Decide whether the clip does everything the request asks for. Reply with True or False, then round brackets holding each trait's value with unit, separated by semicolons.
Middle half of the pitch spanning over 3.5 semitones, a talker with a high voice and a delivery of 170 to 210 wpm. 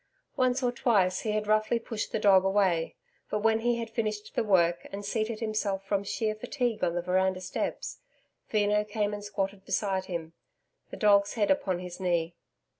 False (2.4 semitones; 205 Hz; 185 wpm)